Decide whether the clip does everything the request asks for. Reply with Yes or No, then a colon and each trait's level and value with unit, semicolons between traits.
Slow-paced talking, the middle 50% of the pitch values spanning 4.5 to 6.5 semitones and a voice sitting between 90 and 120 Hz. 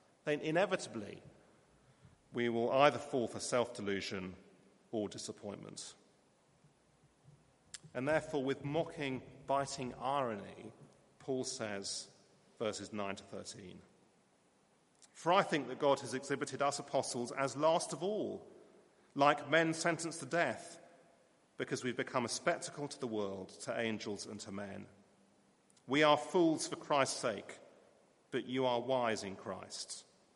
No: slow, 130 wpm; average, 5.1 semitones; low, 130 Hz